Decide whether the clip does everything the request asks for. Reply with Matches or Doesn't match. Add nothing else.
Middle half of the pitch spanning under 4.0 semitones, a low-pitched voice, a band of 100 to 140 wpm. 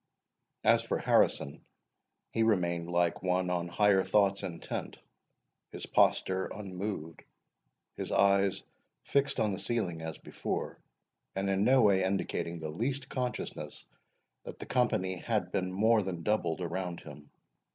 Matches